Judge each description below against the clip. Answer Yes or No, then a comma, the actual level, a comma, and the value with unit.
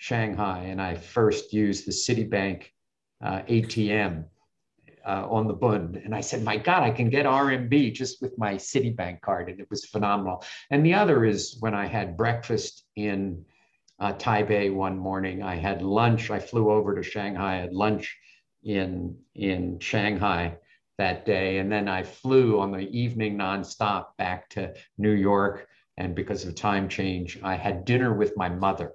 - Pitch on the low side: Yes, low, 100 Hz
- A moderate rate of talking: Yes, average, 170 wpm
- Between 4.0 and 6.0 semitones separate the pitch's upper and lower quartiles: No, average, 2.8 semitones